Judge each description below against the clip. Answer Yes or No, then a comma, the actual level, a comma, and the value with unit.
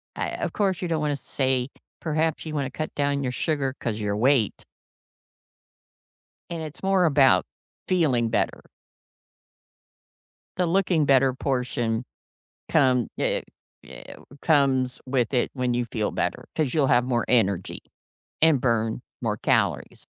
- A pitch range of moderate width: Yes, average, 4.2 semitones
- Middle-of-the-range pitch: No, low, 130 Hz